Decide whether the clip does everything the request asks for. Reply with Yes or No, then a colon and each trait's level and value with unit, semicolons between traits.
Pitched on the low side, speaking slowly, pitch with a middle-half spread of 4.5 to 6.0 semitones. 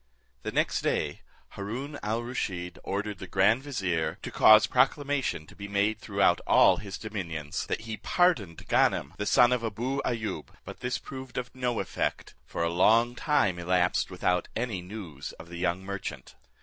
No: low, 105 Hz; average, 170 wpm; average, 5.3 semitones